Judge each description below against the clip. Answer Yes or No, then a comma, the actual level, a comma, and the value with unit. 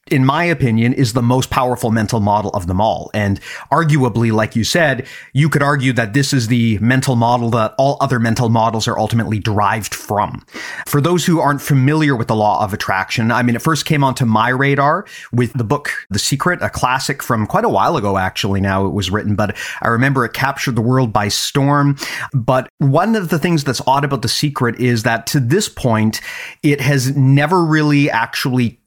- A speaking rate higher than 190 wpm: Yes, fast, 205 wpm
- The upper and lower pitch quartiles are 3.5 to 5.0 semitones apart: Yes, average, 4.0 semitones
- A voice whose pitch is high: No, low, 125 Hz